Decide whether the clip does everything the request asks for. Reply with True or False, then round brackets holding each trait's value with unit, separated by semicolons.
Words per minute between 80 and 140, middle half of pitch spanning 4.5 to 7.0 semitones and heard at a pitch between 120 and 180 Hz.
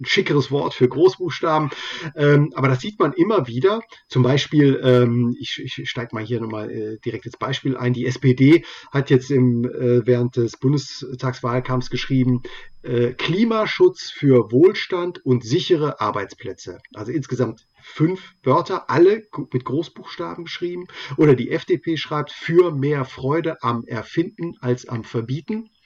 True (130 wpm; 4.8 semitones; 135 Hz)